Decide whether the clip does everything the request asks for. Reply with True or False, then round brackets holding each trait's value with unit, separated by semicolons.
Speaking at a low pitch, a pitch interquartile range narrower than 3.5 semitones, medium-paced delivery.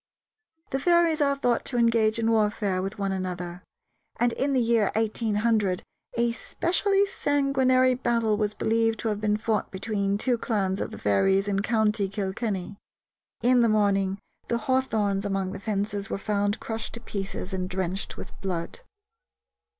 False (215 Hz; 3.1 semitones; 160 wpm)